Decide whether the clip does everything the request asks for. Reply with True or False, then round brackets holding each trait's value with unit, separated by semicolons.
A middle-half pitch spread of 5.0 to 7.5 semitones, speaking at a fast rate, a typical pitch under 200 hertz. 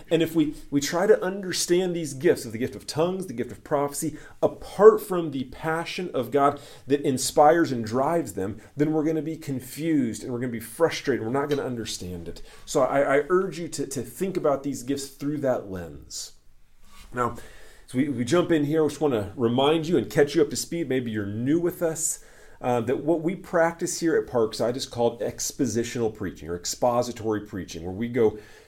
True (5.6 semitones; 220 wpm; 140 Hz)